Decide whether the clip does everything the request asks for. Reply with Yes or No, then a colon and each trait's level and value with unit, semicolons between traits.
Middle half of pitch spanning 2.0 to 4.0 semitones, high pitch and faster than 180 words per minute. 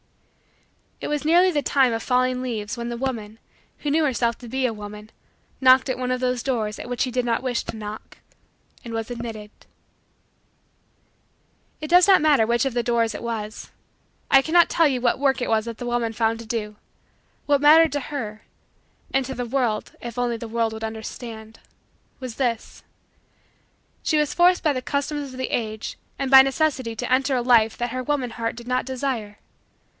Yes: average, 3.0 semitones; high, 245 Hz; average, 200 wpm